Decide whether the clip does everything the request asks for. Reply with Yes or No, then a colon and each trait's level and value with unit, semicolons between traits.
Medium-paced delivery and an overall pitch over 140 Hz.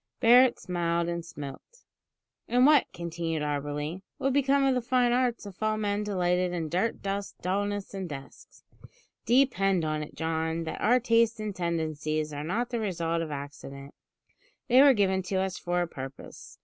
Yes: average, 170 wpm; medium, 185 Hz